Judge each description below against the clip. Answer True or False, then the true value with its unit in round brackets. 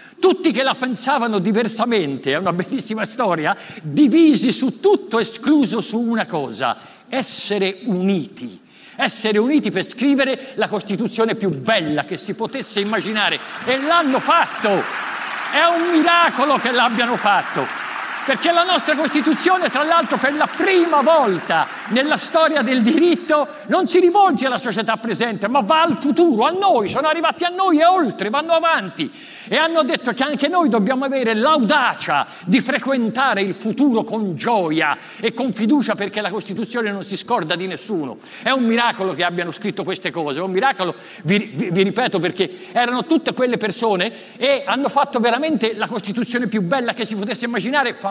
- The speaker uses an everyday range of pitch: False (6.0 semitones)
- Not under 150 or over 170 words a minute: True (165 wpm)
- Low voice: False (245 Hz)